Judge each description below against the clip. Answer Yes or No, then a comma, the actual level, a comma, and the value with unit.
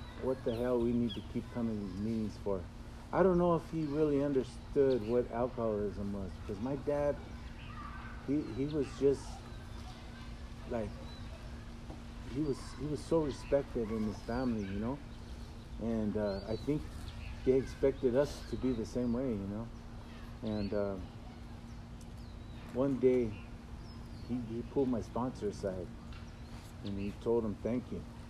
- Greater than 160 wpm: No, average, 145 wpm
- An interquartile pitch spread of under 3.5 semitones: Yes, average, 2.9 semitones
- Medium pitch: No, low, 115 Hz